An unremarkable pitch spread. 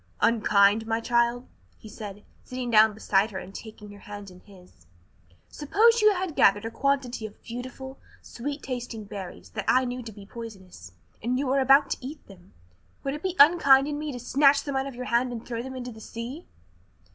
Yes: average, 4.4 semitones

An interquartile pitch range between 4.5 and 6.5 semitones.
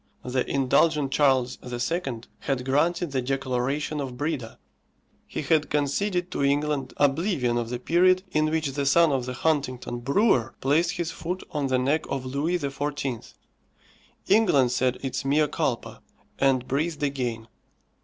No: average, 3.5 semitones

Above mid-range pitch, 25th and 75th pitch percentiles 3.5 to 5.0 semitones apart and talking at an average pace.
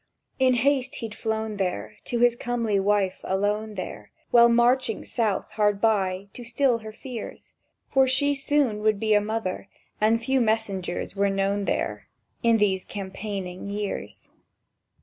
No: high, 215 Hz; average, 3.0 semitones; average, 150 wpm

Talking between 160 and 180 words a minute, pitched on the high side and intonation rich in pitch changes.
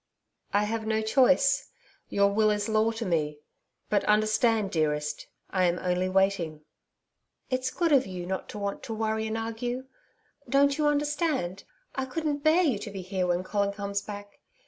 No: average, 170 wpm; high, 215 Hz; average, 5.0 semitones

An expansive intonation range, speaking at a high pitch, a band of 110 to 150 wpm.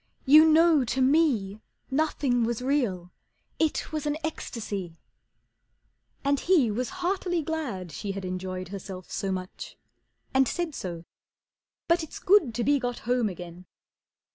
Yes: wide, 8.2 semitones; very high, 250 Hz; average, 140 wpm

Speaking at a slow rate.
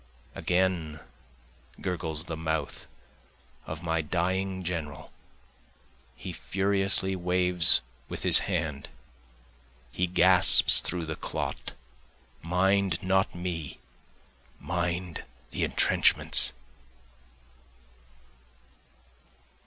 Yes: slow, 75 wpm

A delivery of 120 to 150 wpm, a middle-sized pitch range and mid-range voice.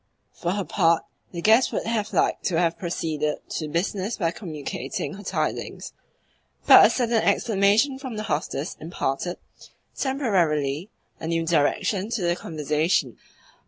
Yes: average, 145 wpm; average, 5.0 semitones; medium, 175 Hz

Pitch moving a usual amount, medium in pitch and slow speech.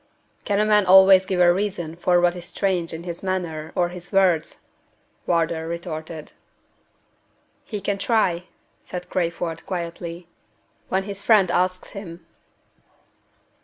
No: narrow, 2.2 semitones; medium, 180 Hz; slow, 130 wpm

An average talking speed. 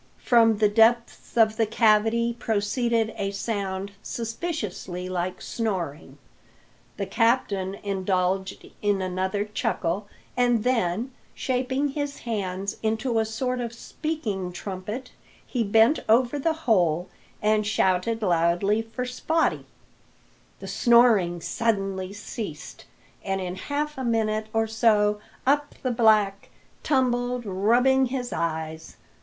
No: slow, 115 wpm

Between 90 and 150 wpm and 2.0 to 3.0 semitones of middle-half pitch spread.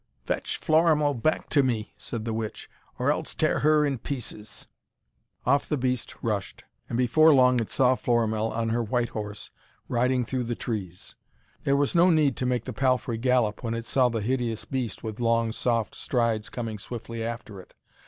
No: average, 185 wpm; narrow, 2.5 semitones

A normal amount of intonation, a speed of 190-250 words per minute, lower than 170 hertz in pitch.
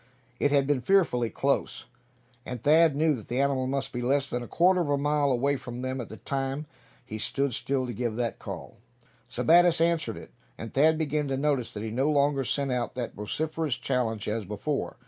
Yes: average, 3.3 semitones; fast, 205 wpm; low, 135 Hz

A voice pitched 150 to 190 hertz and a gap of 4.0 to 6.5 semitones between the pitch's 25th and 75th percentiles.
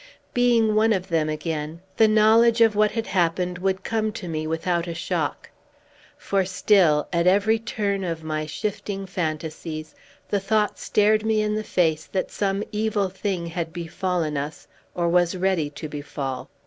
Yes: medium, 185 Hz; average, 4.6 semitones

